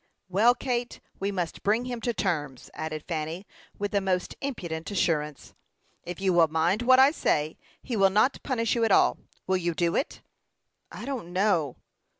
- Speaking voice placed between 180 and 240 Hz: Yes, high, 190 Hz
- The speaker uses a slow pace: No, average, 175 wpm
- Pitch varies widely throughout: Yes, wide, 5.9 semitones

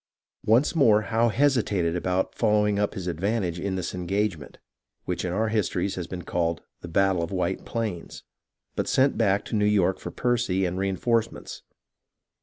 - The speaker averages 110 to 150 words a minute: No, average, 170 wpm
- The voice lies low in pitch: Yes, low, 100 Hz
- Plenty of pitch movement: No, average, 3.7 semitones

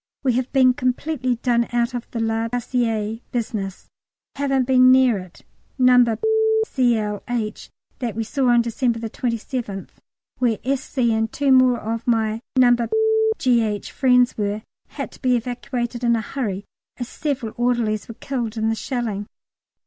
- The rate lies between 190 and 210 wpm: No, average, 150 wpm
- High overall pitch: Yes, high, 240 Hz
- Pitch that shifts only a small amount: Yes, narrow, 2.3 semitones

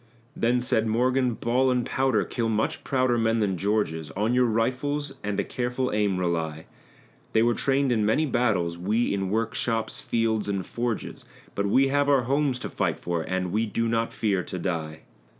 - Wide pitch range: No, average, 3.9 semitones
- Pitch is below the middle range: Yes, low, 115 Hz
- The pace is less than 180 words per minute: No, average, 185 wpm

